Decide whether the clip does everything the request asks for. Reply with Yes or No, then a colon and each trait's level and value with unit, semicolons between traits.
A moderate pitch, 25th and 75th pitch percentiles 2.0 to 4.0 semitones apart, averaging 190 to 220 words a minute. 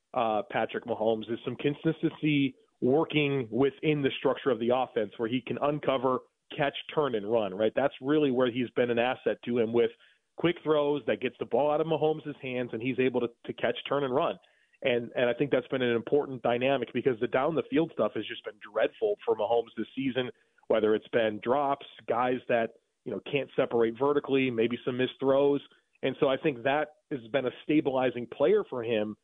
No: low, 130 Hz; average, 3.5 semitones; fast, 205 wpm